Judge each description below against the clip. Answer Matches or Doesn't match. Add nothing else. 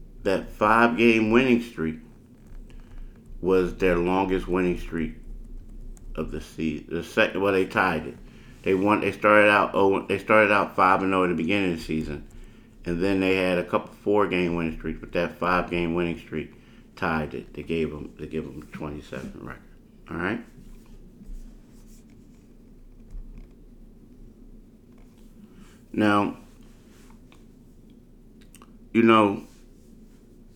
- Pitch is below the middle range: Matches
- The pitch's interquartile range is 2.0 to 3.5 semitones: Doesn't match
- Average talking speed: Doesn't match